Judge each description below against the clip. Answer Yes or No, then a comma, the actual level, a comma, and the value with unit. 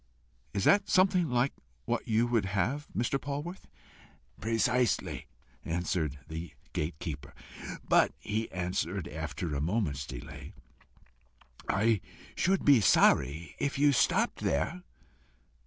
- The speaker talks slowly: Yes, slow, 115 wpm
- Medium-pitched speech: No, low, 105 Hz